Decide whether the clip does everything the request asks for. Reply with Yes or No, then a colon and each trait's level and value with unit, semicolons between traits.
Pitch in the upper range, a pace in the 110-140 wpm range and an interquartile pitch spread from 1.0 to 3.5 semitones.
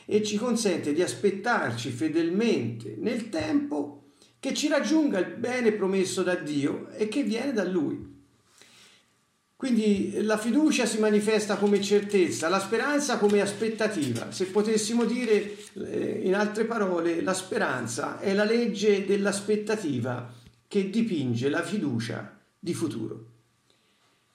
No: high, 205 Hz; average, 125 wpm; average, 4.0 semitones